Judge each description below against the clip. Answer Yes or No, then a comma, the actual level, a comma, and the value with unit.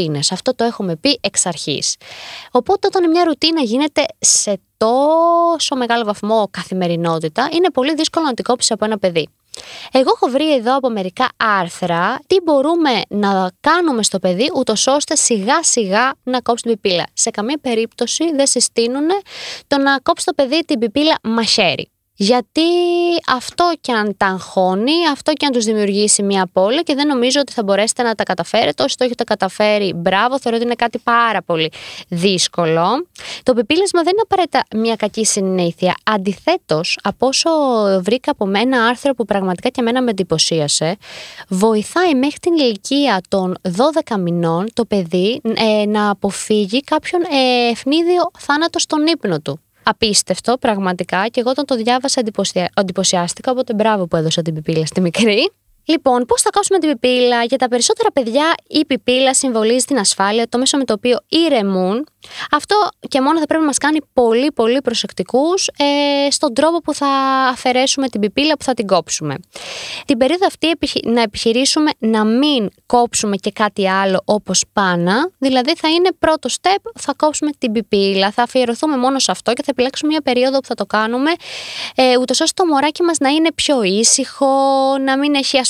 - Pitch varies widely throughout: Yes, wide, 5.9 semitones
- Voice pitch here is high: Yes, high, 245 Hz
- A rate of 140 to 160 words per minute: No, fast, 170 wpm